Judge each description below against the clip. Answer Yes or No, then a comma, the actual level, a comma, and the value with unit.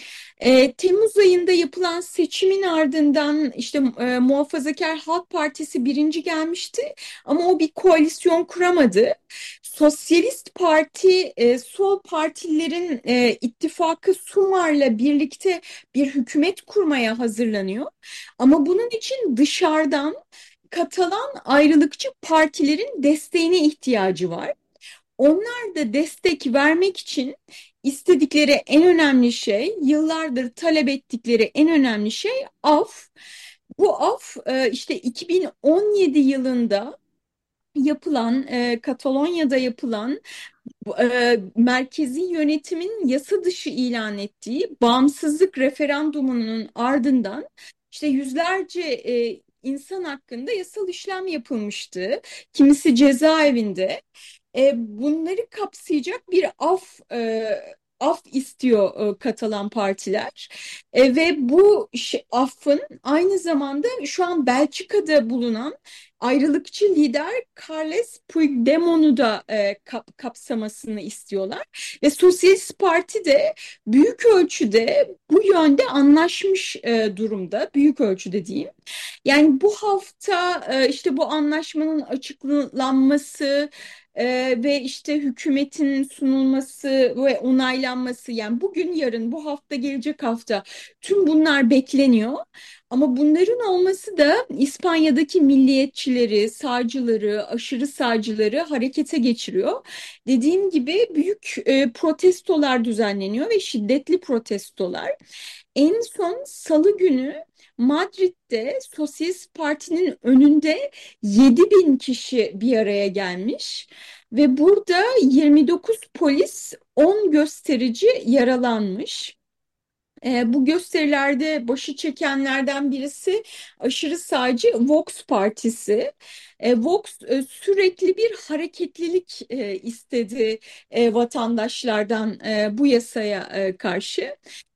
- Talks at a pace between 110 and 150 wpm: No, slow, 95 wpm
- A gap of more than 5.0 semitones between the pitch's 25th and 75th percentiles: Yes, wide, 5.6 semitones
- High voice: Yes, very high, 290 Hz